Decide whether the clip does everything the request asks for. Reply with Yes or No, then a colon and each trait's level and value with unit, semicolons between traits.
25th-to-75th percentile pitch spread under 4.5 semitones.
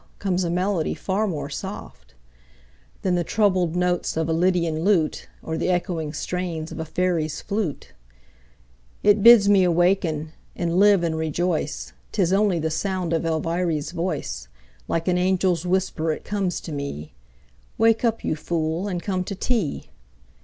Yes: average, 2.8 semitones